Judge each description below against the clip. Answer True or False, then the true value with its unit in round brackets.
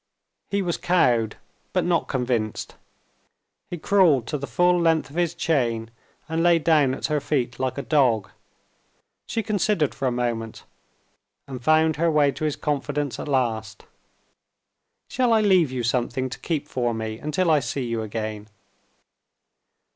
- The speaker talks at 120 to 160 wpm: True (155 wpm)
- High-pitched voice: False (140 Hz)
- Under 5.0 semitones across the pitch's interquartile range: False (5.5 semitones)